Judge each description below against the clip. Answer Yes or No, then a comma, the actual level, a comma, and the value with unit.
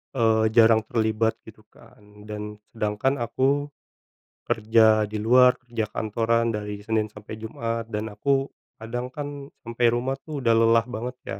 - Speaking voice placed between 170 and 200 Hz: No, low, 115 Hz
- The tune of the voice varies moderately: No, narrow, 2.2 semitones